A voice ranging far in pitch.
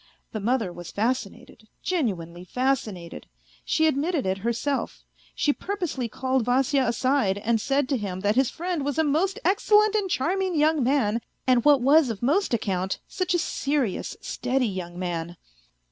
Yes: wide, 6.6 semitones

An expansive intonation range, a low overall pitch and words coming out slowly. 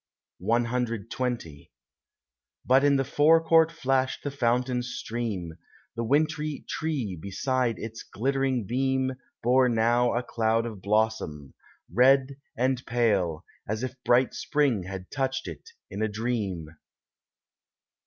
No: average, 3.3 semitones; low, 120 Hz; slow, 115 wpm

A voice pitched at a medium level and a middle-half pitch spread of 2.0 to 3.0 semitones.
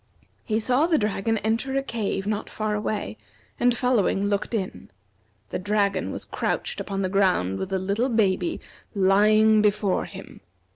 No: high, 210 Hz; narrow, 2.4 semitones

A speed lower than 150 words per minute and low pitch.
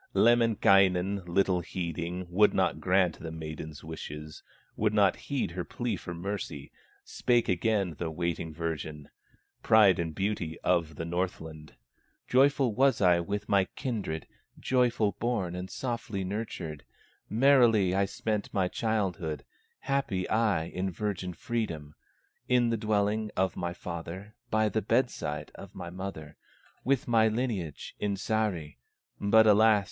Yes: slow, 135 wpm; very low, 95 Hz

